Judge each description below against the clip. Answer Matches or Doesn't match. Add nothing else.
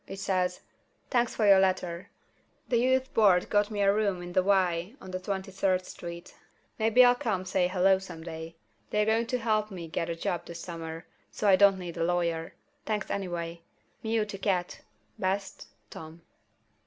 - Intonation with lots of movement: Doesn't match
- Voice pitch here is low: Doesn't match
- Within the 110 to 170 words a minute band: Doesn't match